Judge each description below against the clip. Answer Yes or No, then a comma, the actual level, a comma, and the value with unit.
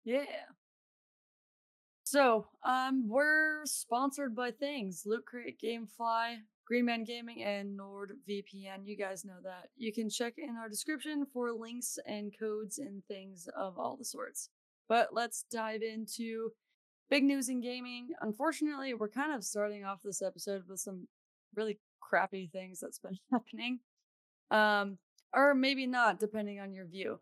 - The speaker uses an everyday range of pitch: Yes, average, 4.1 semitones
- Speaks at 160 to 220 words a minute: No, average, 150 wpm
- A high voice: Yes, high, 225 Hz